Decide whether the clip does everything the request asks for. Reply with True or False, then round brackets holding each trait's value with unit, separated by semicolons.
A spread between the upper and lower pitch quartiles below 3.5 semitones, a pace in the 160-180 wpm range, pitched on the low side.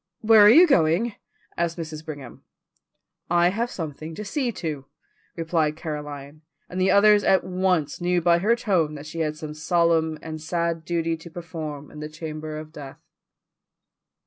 False (2.7 semitones; 165 wpm; 165 Hz)